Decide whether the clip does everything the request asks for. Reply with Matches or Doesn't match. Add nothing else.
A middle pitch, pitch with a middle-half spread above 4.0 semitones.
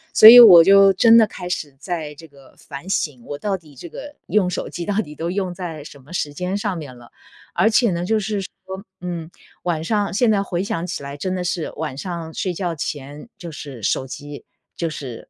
Matches